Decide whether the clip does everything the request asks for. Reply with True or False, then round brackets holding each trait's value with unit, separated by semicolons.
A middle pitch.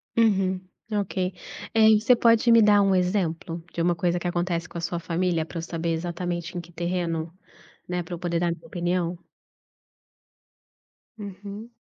True (175 Hz)